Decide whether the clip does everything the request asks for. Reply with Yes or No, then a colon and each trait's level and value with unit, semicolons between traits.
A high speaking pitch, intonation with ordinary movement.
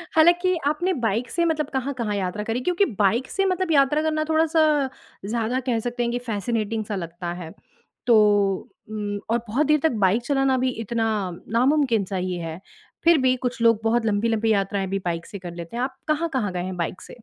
No: high, 235 Hz; wide, 6.3 semitones